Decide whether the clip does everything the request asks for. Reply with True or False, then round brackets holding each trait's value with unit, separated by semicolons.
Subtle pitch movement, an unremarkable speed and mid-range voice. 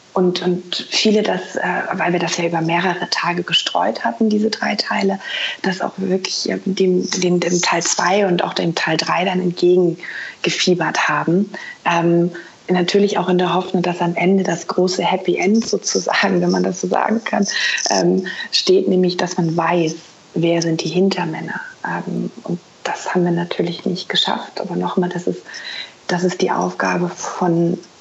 True (1.8 semitones; 175 wpm; 180 Hz)